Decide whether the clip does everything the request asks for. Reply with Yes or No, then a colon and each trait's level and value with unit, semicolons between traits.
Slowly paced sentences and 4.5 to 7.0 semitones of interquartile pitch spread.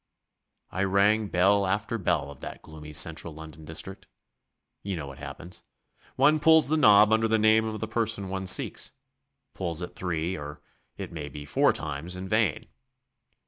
No: average, 170 wpm; wide, 5.5 semitones